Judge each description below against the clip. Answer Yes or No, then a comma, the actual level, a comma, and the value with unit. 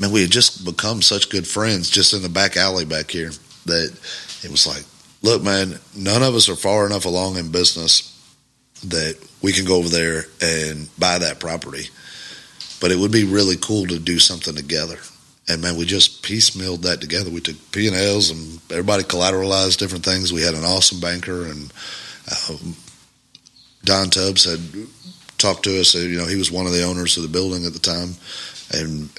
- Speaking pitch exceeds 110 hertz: No, very low, 90 Hz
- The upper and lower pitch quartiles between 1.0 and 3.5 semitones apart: Yes, average, 2.7 semitones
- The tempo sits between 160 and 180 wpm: No, average, 190 wpm